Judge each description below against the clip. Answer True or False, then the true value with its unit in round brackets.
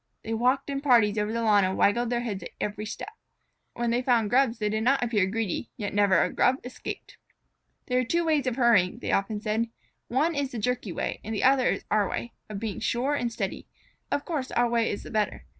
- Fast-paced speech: True (230 wpm)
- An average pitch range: True (3.2 semitones)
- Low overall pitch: False (235 Hz)